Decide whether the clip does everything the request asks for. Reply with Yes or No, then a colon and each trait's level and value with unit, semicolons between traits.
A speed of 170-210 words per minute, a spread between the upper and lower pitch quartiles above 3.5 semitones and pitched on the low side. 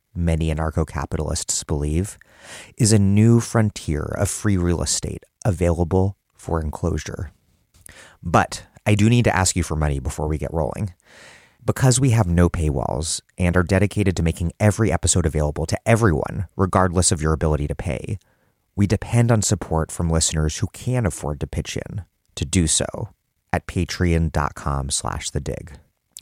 No: average, 155 wpm; average, 4.8 semitones; very low, 90 Hz